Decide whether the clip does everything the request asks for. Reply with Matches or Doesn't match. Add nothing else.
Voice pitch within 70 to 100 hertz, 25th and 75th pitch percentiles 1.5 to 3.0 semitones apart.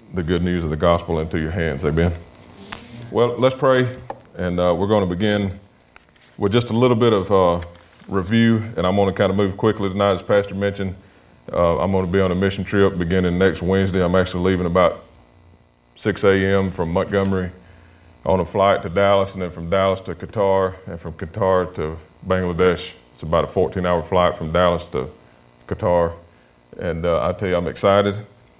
Matches